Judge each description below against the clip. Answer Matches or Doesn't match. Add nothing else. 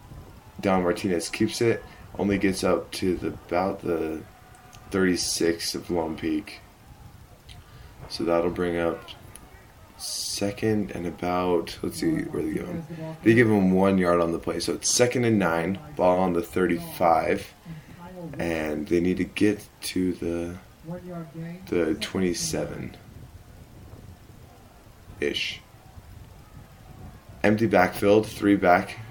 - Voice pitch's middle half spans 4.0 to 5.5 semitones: Matches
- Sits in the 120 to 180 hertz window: Doesn't match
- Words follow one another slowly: Matches